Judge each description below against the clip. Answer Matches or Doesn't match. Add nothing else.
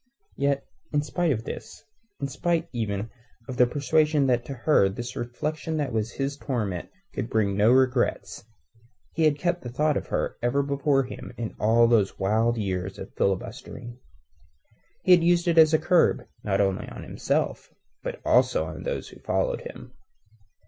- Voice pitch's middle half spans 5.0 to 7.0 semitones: Matches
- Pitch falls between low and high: Doesn't match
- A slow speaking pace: Doesn't match